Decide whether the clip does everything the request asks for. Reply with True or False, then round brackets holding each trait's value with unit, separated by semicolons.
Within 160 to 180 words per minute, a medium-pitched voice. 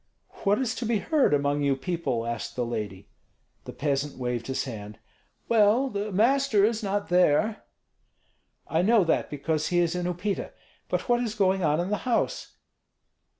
True (170 wpm; 180 Hz)